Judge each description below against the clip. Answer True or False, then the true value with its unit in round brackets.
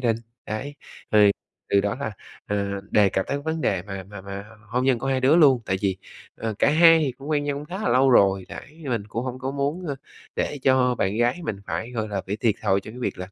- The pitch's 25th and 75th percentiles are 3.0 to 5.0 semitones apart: False (5.6 semitones)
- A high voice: False (120 Hz)